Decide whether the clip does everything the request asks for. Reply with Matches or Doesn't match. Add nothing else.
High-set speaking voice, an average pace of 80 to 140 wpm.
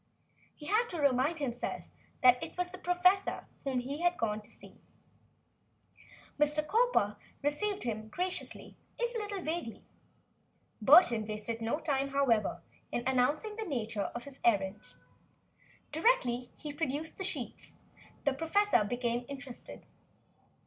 Matches